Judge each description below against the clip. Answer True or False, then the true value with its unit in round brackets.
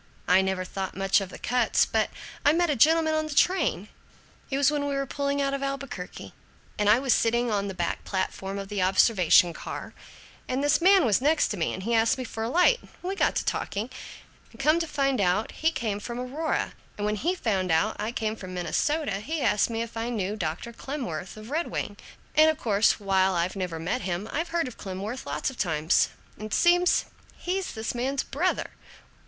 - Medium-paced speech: False (215 wpm)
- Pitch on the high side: True (230 Hz)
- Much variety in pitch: True (6.8 semitones)